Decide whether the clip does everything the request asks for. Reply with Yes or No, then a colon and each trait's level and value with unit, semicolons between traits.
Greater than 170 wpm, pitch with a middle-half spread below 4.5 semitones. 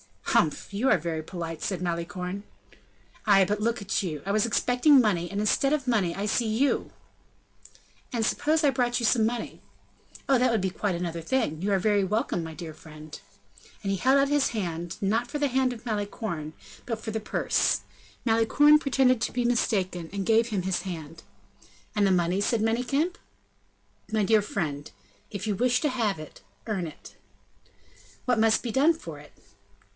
No: average, 180 wpm; wide, 5.4 semitones